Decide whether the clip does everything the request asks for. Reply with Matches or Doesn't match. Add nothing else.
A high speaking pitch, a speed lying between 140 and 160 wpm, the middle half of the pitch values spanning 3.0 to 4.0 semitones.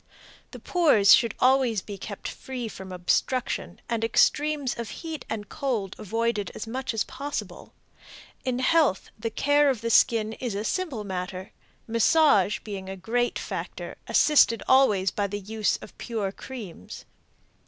Doesn't match